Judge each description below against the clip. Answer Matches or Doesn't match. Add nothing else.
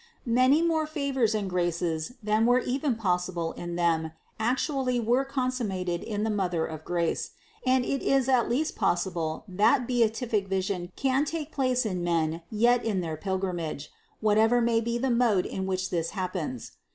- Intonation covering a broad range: Matches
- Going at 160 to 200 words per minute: Matches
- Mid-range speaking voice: Doesn't match